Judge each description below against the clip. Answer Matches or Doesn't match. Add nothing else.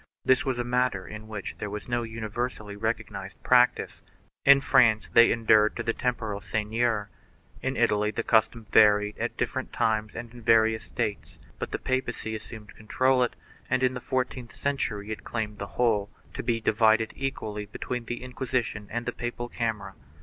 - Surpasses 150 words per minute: Matches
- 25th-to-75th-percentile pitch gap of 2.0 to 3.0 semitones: Matches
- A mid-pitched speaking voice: Doesn't match